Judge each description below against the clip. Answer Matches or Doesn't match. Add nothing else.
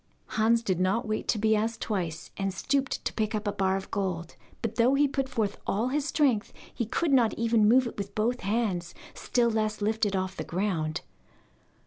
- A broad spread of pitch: Doesn't match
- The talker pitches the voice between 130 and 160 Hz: Doesn't match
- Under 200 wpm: Doesn't match